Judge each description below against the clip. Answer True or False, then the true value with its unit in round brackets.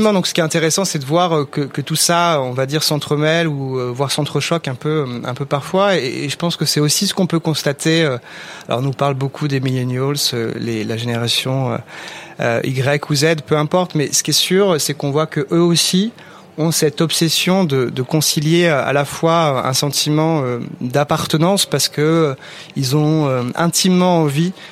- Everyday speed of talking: True (185 wpm)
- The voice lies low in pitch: False (150 Hz)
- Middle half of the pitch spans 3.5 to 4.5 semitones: False (3.1 semitones)